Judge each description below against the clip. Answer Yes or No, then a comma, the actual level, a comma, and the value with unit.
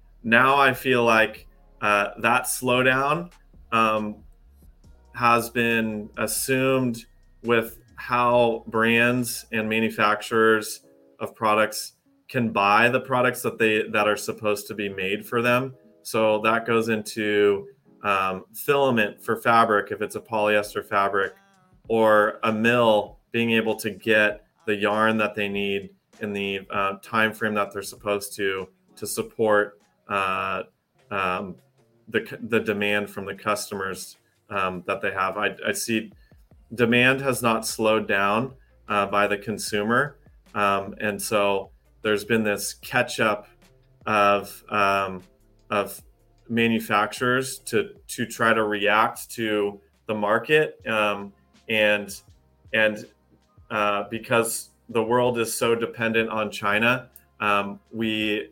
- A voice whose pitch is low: Yes, low, 110 Hz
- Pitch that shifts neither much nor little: No, narrow, 2.3 semitones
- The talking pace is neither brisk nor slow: No, slow, 130 wpm